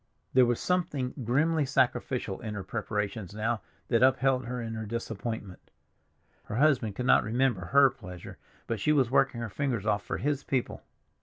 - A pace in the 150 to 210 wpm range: Yes, average, 170 wpm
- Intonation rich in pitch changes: No, average, 3.7 semitones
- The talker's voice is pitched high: No, low, 120 Hz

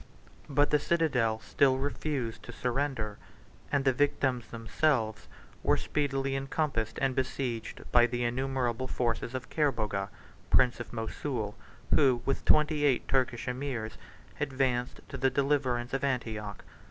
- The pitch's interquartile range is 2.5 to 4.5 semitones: Yes, average, 2.8 semitones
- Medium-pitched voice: No, low, 130 Hz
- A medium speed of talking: No, slow, 130 wpm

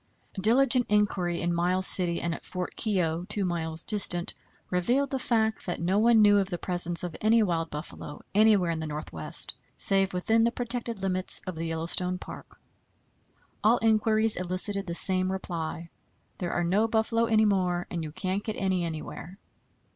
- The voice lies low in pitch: No, medium, 185 Hz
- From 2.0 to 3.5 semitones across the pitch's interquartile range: No, average, 3.9 semitones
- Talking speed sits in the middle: Yes, average, 170 wpm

